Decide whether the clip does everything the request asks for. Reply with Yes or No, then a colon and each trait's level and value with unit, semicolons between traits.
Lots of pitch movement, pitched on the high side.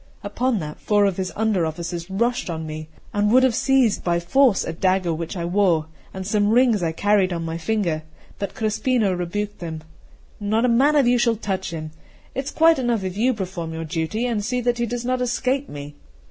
Yes: wide, 5.9 semitones; high, 205 Hz